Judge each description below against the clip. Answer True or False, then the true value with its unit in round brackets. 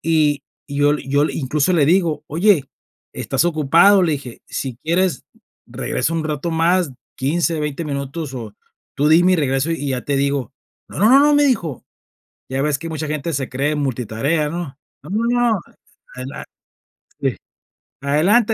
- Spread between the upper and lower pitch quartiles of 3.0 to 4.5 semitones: True (3.5 semitones)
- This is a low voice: False (150 Hz)